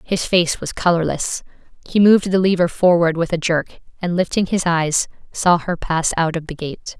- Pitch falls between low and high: Yes, medium, 170 Hz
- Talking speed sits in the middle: Yes, average, 195 wpm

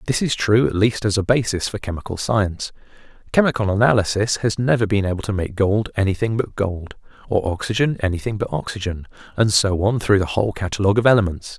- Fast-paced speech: No, average, 190 wpm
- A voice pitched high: No, low, 105 Hz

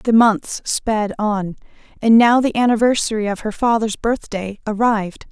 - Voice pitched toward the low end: No, high, 220 Hz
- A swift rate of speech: No, average, 145 wpm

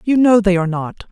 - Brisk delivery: Yes, fast, 270 wpm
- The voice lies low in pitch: No, high, 200 Hz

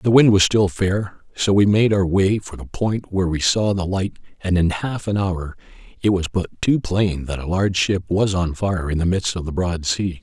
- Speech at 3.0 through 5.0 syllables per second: Yes, 4.8 syllables/s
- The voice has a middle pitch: No, very low, 95 Hz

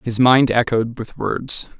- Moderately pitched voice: No, low, 120 Hz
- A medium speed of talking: Yes, average, 165 wpm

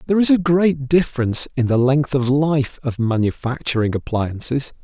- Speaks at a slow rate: No, average, 160 wpm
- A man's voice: Yes, male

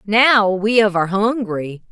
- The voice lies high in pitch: Yes, high, 205 Hz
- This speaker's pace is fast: No, average, 155 wpm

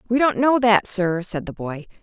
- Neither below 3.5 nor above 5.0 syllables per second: Yes, 4.7 syllables/s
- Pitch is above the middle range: Yes, high, 210 Hz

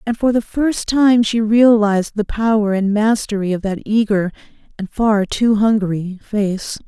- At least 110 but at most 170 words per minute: Yes, average, 165 wpm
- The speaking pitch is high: Yes, high, 215 Hz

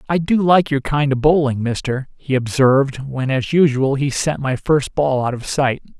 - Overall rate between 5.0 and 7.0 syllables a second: No, 4.7 syllables/s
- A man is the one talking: Yes, male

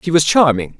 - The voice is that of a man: Yes, male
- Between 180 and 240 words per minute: Yes, fast, 230 wpm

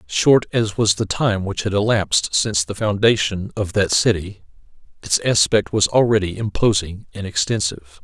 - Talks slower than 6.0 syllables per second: Yes, 4.9 syllables/s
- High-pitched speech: No, low, 100 Hz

